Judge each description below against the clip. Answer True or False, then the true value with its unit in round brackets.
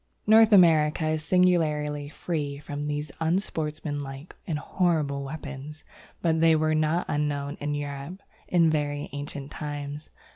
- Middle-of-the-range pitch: True (150 Hz)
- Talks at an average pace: False (125 wpm)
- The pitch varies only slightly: True (2.0 semitones)